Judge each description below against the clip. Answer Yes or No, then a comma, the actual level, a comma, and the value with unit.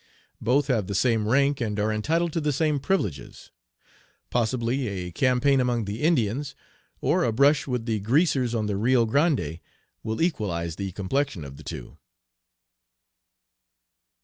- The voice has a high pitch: No, low, 120 Hz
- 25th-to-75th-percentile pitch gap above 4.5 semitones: Yes, average, 5.1 semitones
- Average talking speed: Yes, average, 150 wpm